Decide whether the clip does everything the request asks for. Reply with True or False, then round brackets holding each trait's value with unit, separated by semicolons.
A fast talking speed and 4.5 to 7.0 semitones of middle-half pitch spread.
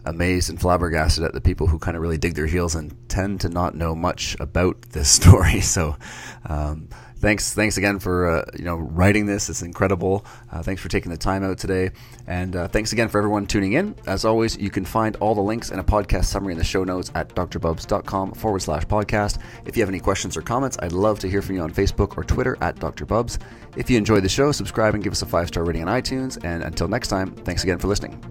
False (240 wpm; 3.4 semitones)